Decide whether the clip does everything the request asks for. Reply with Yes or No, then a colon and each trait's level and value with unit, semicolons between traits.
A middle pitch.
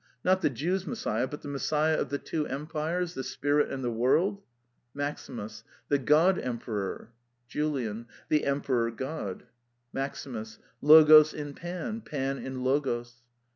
Yes: medium, 145 Hz